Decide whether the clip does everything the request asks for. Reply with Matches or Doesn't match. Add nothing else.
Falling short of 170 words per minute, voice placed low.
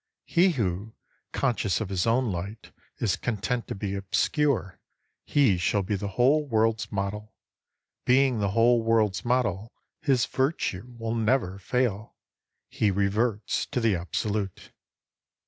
Matches